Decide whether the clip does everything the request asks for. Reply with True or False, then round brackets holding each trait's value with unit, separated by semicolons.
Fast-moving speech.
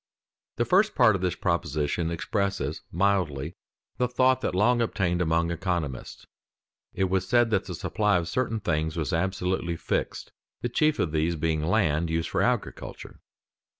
False (160 wpm)